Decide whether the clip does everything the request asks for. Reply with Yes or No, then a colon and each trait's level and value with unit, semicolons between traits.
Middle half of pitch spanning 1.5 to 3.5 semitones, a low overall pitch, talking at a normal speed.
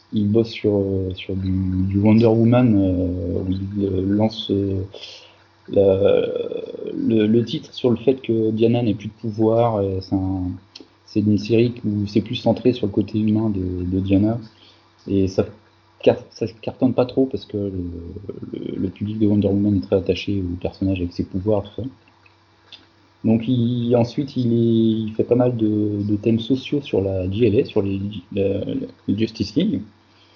Yes: average, 3.1 semitones; low, 105 Hz; average, 170 wpm